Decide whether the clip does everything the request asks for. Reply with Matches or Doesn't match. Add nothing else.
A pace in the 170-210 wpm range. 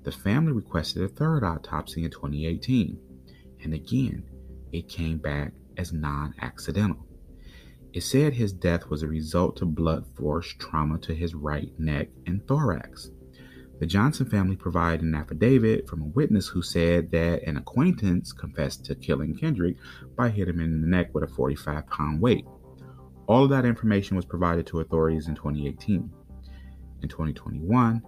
Doesn't match